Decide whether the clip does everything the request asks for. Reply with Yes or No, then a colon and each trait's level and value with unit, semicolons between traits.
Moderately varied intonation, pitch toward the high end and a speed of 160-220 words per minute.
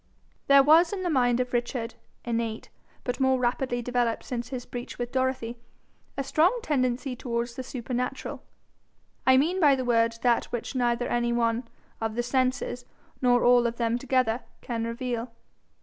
No: narrow, 1.6 semitones; high, 245 Hz; average, 165 wpm